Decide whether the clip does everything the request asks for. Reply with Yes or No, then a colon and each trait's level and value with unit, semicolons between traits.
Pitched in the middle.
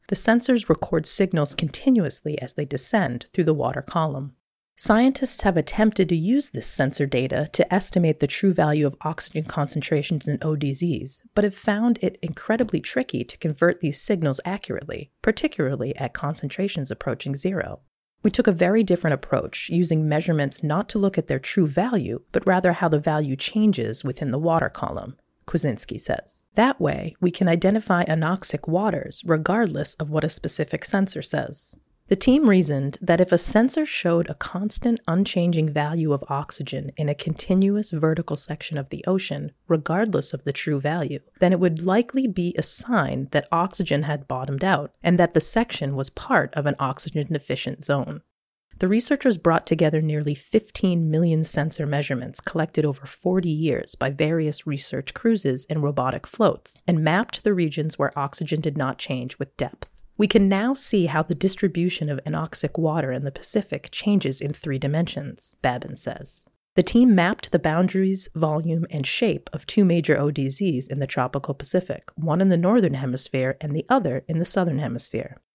Yes: medium, 160 Hz